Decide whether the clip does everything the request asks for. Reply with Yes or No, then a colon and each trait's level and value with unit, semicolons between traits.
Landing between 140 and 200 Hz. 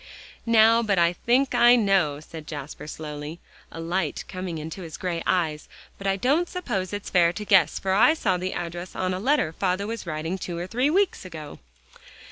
Yes: medium, 185 Hz